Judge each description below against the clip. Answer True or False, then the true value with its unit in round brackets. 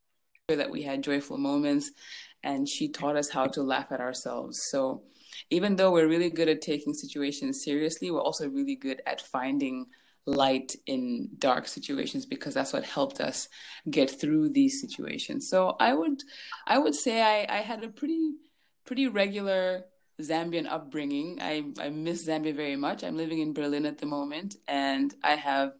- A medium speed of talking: True (170 wpm)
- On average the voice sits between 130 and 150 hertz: False (185 Hz)